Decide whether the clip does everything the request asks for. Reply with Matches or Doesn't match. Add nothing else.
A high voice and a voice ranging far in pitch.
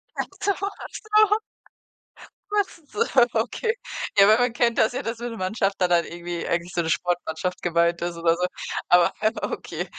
Matches